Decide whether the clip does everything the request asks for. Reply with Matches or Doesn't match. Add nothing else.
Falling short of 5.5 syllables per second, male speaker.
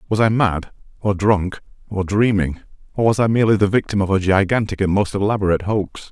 Doesn't match